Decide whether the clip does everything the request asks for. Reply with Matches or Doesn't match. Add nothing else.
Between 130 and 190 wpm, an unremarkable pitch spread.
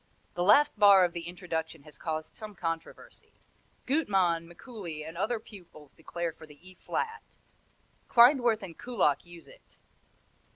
Matches